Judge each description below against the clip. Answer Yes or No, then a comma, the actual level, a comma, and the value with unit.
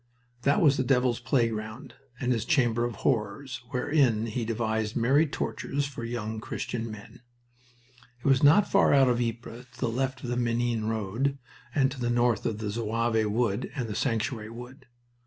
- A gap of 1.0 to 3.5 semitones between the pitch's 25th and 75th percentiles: Yes, average, 2.9 semitones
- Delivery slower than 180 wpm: Yes, average, 170 wpm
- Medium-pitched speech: No, low, 120 Hz